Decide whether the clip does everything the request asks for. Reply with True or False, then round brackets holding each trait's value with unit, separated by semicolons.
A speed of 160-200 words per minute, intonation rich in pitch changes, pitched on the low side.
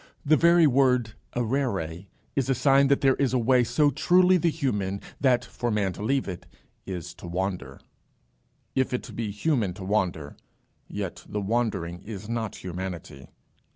True (165 wpm; 6.1 semitones; 115 Hz)